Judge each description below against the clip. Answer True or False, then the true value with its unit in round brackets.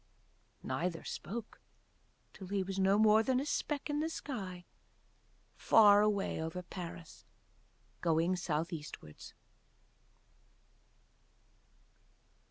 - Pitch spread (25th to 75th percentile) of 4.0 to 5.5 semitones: True (4.3 semitones)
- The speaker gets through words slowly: True (95 wpm)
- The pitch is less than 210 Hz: True (190 Hz)